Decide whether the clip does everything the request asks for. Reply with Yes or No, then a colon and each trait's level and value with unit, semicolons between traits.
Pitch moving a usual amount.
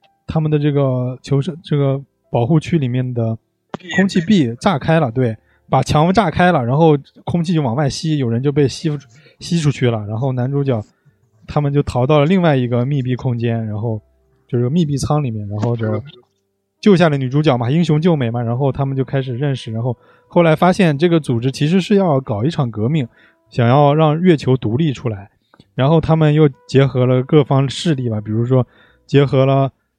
Yes: average, 4.4 semitones